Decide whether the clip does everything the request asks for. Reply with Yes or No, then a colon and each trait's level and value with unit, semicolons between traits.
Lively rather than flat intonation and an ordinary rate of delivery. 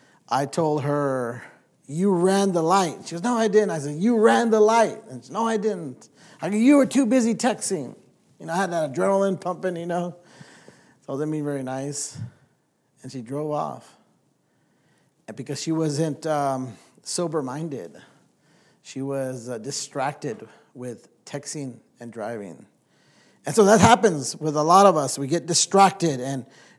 Yes: wide, 6.0 semitones; average, 170 wpm